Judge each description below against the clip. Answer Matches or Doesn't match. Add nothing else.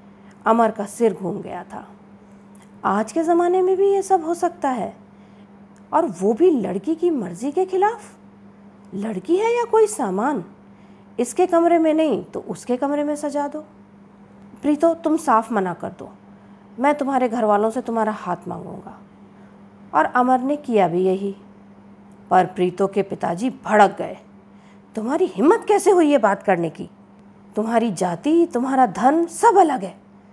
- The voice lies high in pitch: Matches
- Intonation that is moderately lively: Doesn't match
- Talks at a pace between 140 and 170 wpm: Matches